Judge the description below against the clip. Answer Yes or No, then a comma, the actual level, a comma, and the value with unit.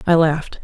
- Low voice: No, medium, 160 Hz